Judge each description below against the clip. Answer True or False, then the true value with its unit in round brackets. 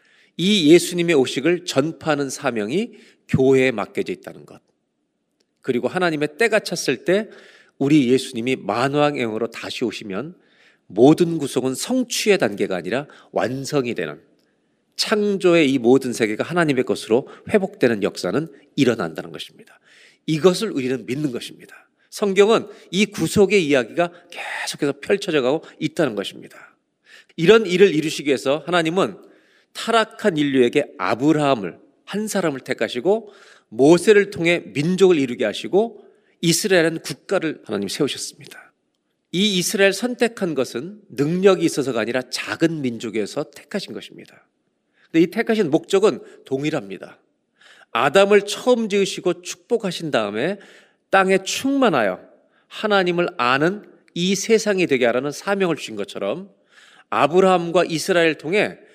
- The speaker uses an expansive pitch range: True (6.5 semitones)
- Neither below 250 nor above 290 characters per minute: False (320 characters per minute)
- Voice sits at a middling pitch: True (165 Hz)